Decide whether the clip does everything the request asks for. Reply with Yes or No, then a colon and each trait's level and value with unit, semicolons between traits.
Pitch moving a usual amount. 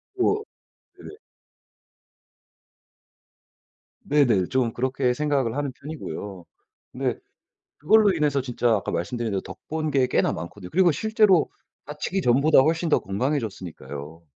No: wide, 6.1 semitones